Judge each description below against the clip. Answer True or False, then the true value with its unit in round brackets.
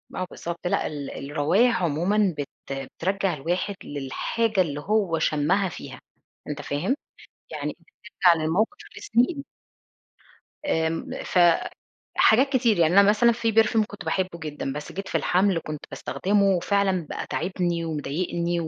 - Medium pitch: True (180 Hz)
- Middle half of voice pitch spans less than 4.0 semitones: False (4.5 semitones)